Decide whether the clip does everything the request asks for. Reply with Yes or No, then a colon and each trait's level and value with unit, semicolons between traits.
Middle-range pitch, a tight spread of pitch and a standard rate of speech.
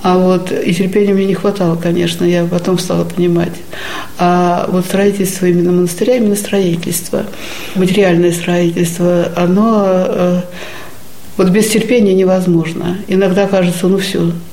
Yes: medium, 180 Hz; narrow, 1.8 semitones; average, 125 wpm